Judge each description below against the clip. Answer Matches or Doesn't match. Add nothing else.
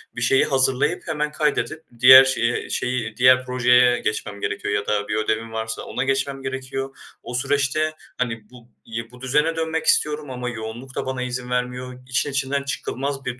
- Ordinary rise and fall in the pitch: Doesn't match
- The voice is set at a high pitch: Doesn't match